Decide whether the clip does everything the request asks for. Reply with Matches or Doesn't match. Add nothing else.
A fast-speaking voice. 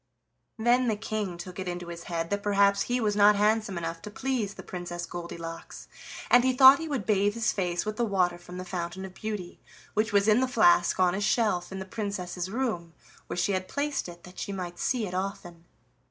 Matches